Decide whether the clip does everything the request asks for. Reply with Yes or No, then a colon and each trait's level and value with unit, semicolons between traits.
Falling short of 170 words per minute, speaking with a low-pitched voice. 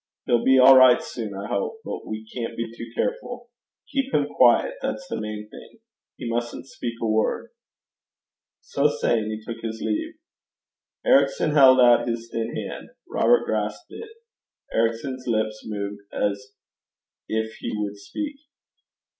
Yes: average, 150 wpm; low, 115 Hz